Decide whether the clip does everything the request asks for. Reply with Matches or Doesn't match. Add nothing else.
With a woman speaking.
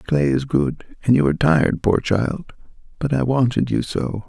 Doesn't match